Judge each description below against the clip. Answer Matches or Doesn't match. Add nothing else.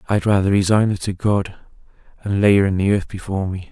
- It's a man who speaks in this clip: Matches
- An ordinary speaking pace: Doesn't match